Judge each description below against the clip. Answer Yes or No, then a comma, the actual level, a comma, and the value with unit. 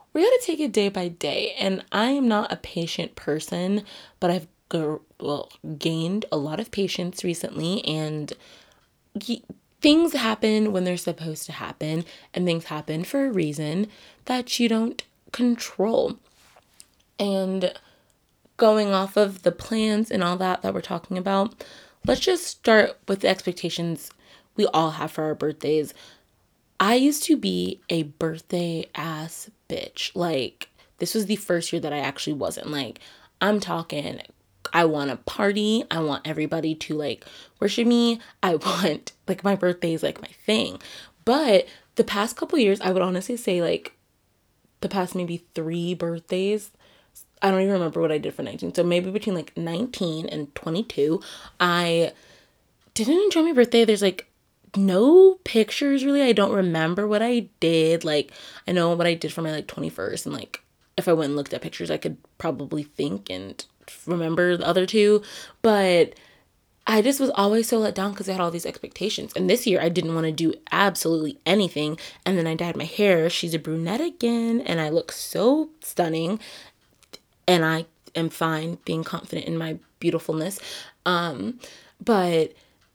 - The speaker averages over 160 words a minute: Yes, average, 170 wpm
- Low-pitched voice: No, medium, 180 Hz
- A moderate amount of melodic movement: Yes, average, 4.7 semitones